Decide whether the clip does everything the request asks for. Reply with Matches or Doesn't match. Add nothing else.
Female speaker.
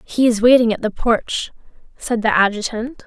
Matches